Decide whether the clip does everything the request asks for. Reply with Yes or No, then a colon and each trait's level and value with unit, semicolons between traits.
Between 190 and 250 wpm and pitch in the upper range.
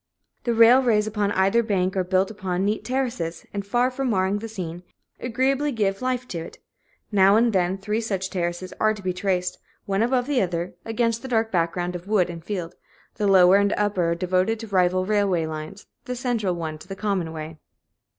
Yes: average, 195 wpm; high, 195 Hz